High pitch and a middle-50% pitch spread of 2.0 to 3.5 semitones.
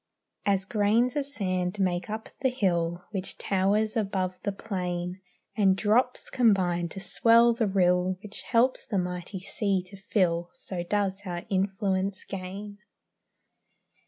Yes: high, 195 Hz; narrow, 2.6 semitones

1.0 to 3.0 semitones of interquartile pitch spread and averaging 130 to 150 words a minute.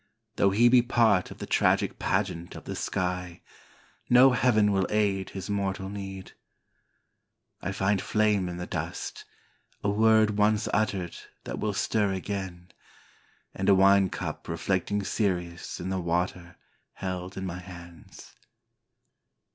Yes: narrow, 2.4 semitones; average, 140 wpm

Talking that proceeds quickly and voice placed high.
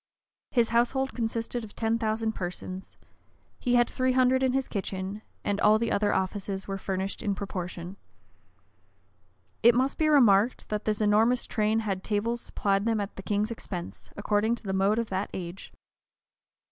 No: average, 165 wpm; high, 215 Hz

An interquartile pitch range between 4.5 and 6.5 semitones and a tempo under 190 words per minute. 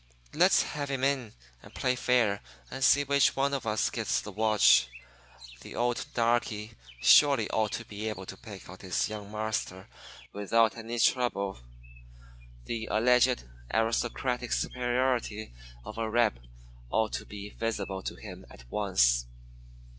No: average, 3.1 semitones; average, 140 wpm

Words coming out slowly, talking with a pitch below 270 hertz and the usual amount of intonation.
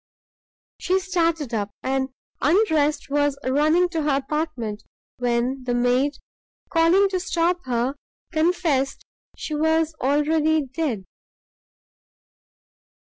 No: slow, 100 wpm; very high, 295 Hz; average, 3.9 semitones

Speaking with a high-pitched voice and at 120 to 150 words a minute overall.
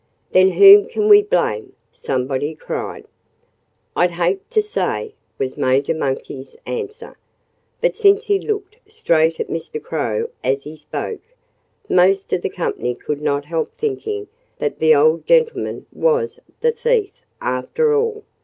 Yes: very high, 395 Hz; average, 140 wpm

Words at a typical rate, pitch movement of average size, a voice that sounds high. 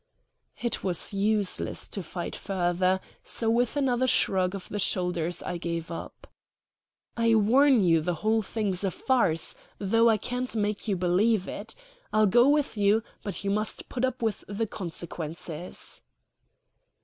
Yes: average, 150 wpm; average, 4.2 semitones; high, 205 Hz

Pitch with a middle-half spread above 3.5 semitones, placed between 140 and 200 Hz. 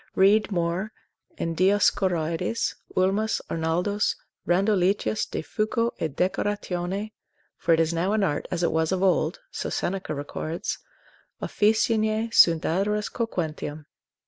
Yes: average, 4.0 semitones; medium, 185 Hz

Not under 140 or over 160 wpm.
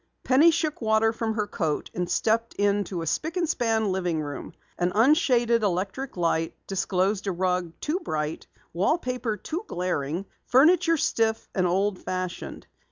Yes: average, 150 wpm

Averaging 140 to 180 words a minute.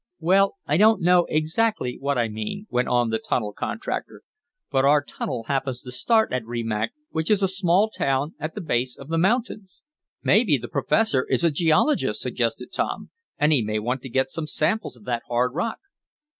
No: average, 190 wpm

